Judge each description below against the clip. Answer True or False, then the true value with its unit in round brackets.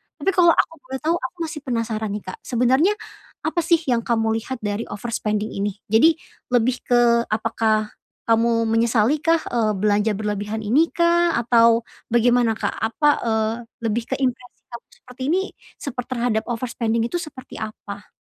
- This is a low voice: False (235 Hz)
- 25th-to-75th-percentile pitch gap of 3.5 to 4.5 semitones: False (2.8 semitones)